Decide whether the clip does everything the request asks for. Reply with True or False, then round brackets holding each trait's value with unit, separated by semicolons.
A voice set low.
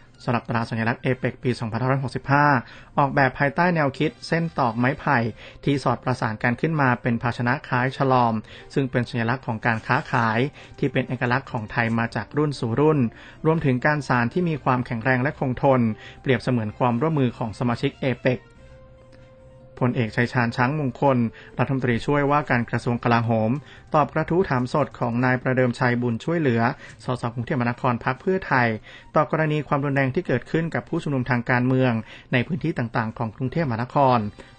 True (130 Hz)